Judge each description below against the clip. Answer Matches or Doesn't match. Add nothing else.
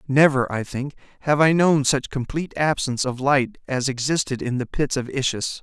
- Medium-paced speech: Matches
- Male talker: Matches